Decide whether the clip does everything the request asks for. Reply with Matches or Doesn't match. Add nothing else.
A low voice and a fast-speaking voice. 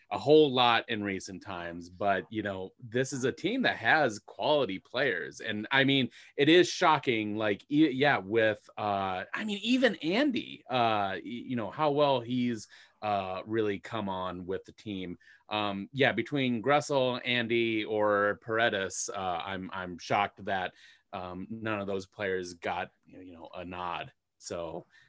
Doesn't match